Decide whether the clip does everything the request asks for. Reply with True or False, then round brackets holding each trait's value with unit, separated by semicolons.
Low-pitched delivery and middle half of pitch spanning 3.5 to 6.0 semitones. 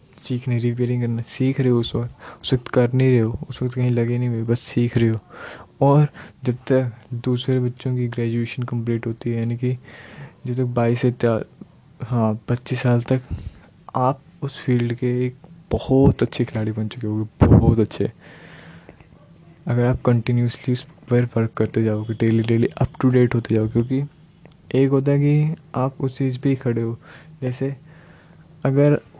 False (125 Hz; 2.5 semitones)